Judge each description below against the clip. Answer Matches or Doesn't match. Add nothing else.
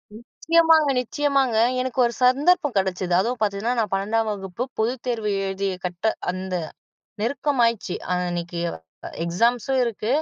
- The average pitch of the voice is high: Matches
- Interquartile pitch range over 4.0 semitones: Matches